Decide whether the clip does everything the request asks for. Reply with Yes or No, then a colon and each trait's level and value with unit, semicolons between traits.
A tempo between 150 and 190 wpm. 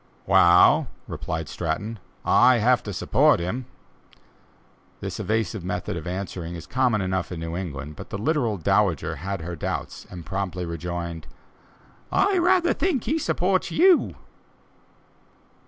No: slow, 135 wpm